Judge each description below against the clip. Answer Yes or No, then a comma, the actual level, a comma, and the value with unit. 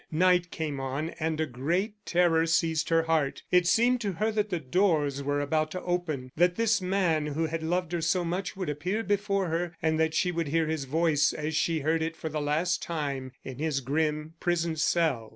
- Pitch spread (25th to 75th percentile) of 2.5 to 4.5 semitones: Yes, average, 2.8 semitones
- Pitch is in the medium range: Yes, medium, 165 Hz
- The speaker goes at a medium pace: No, fast, 210 wpm